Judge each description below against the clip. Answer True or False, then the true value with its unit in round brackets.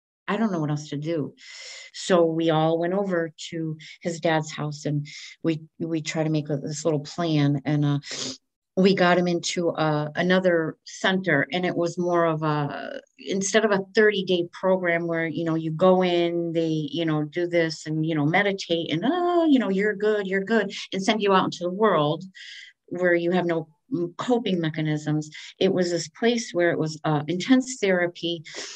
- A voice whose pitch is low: False (170 Hz)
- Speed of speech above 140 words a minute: True (195 wpm)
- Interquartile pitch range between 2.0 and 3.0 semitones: False (3.4 semitones)